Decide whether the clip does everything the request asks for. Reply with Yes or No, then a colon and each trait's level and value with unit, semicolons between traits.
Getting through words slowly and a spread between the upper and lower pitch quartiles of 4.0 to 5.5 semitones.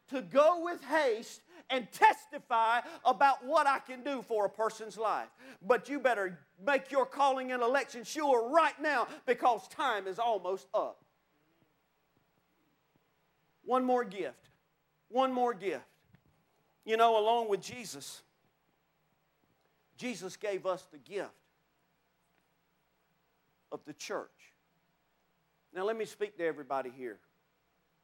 Yes: slow, 120 wpm; average, 5.2 semitones